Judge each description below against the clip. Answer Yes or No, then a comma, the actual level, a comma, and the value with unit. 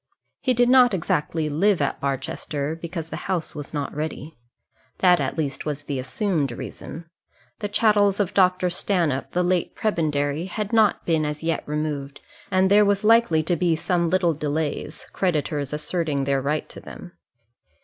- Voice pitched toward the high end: No, medium, 165 Hz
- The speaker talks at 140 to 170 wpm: Yes, average, 165 wpm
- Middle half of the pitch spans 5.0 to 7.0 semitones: No, average, 4.3 semitones